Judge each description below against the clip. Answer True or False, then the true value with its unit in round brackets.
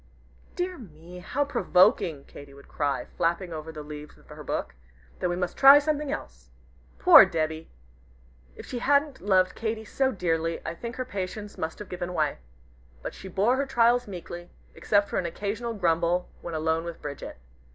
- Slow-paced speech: False (175 wpm)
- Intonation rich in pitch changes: True (6.0 semitones)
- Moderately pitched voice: True (180 Hz)